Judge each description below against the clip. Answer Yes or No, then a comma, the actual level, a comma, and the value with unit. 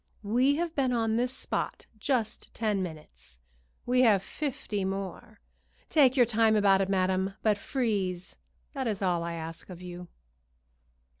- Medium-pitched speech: No, high, 205 Hz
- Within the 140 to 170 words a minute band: Yes, average, 150 wpm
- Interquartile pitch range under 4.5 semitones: No, average, 4.8 semitones